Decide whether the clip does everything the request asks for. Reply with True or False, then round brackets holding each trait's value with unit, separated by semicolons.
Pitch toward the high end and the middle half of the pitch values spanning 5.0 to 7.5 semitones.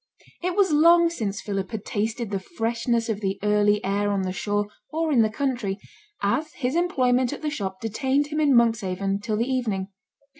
True (225 Hz; 5.6 semitones)